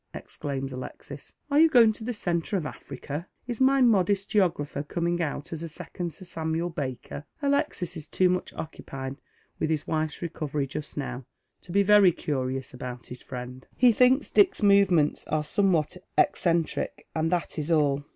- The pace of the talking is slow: No, average, 170 wpm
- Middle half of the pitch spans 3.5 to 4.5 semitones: No, wide, 5.5 semitones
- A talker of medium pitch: Yes, medium, 165 Hz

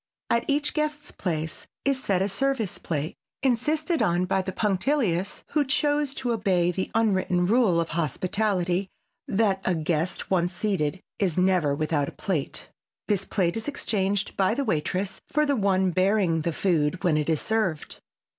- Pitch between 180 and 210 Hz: Yes, high, 190 Hz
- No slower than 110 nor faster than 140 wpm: No, average, 165 wpm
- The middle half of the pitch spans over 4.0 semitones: Yes, average, 4.7 semitones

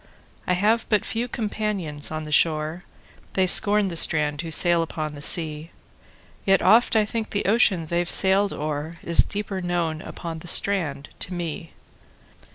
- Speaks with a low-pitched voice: No, medium, 175 Hz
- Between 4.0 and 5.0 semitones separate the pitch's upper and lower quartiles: Yes, average, 4.4 semitones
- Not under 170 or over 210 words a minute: No, average, 150 wpm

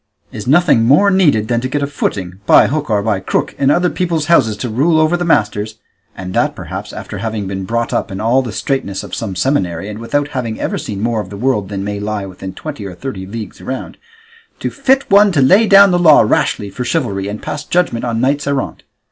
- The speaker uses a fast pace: Yes, fast, 230 wpm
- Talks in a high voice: No, low, 120 Hz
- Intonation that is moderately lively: No, wide, 6.4 semitones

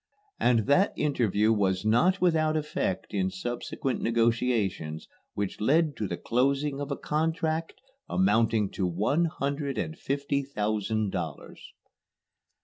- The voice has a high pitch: No, low, 125 Hz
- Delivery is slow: Yes, slow, 125 wpm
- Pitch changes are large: Yes, wide, 6.1 semitones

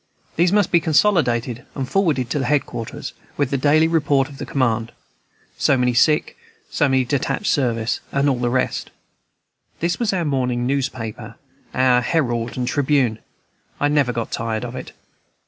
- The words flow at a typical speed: Yes, average, 165 wpm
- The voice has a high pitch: No, low, 130 Hz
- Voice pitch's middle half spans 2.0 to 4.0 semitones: Yes, average, 3.4 semitones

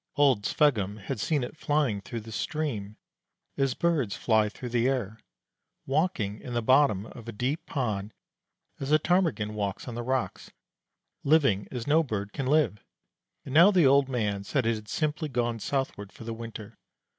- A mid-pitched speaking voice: No, low, 120 Hz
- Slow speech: No, average, 175 wpm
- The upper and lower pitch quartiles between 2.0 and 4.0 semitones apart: No, average, 5.2 semitones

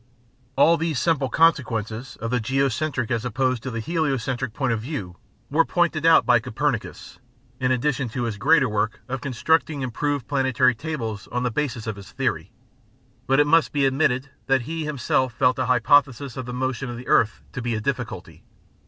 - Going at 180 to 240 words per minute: Yes, average, 185 wpm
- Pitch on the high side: No, low, 130 Hz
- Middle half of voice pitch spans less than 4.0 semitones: Yes, average, 3.5 semitones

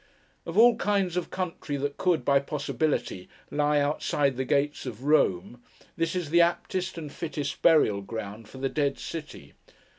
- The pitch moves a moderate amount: Yes, average, 3.8 semitones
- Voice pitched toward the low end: No, medium, 145 Hz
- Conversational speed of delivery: Yes, average, 160 wpm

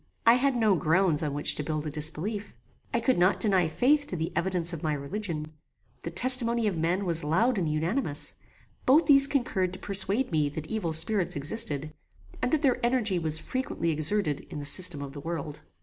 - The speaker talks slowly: No, average, 195 wpm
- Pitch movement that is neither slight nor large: No, wide, 6.7 semitones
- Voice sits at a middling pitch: Yes, medium, 180 Hz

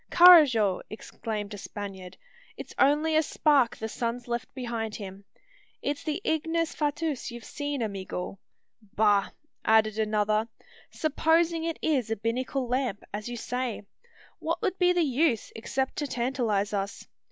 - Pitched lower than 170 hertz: No, high, 240 Hz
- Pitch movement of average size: No, wide, 5.7 semitones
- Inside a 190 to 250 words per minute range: No, average, 140 wpm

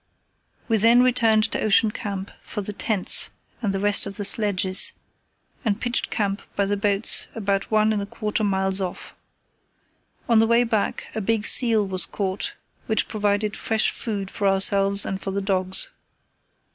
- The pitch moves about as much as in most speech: No, narrow, 1.9 semitones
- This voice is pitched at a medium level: No, high, 205 Hz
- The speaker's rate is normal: Yes, average, 170 wpm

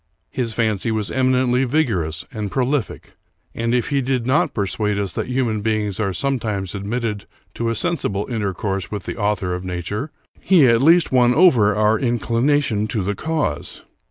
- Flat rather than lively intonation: No, average, 4.0 semitones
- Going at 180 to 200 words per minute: No, average, 165 wpm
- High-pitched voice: No, low, 110 Hz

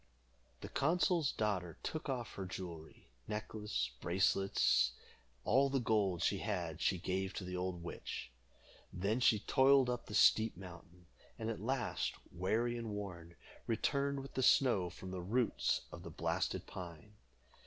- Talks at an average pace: Yes, average, 155 wpm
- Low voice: Yes, low, 100 Hz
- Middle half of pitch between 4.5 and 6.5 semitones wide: Yes, average, 5.1 semitones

